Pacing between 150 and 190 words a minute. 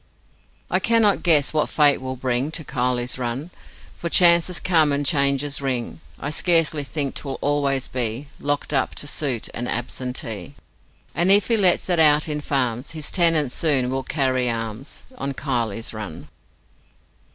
Yes: average, 155 wpm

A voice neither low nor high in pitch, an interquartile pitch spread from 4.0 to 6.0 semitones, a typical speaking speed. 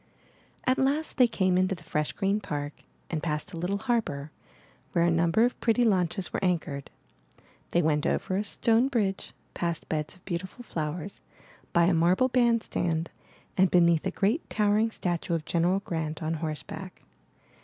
Yes: medium, 180 Hz; average, 4.4 semitones; average, 165 wpm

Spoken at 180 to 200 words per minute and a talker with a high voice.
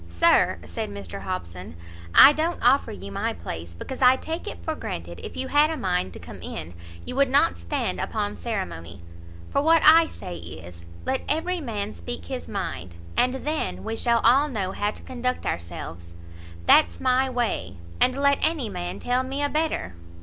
Yes: average, 185 wpm; high, 205 Hz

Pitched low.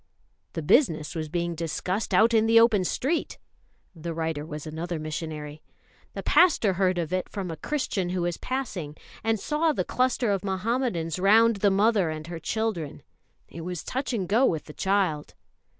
No: medium, 185 Hz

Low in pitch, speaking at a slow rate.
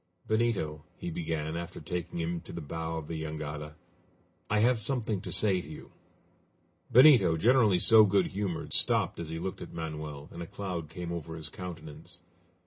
No: very low, 85 Hz; average, 175 wpm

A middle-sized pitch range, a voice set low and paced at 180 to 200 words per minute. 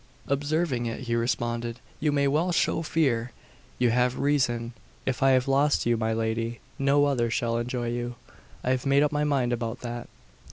Yes: average, 3.1 semitones; low, 125 Hz; average, 185 wpm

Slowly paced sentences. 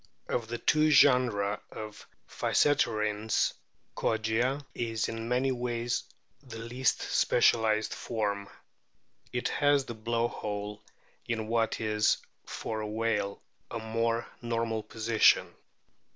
Yes: slow, 110 wpm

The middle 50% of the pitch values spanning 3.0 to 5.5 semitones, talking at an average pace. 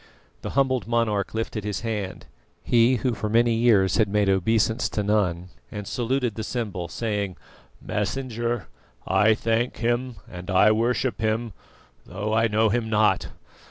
No: narrow, 2.4 semitones; average, 150 wpm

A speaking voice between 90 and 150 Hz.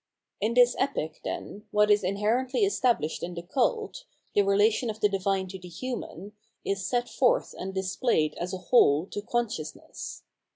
No: high, 205 Hz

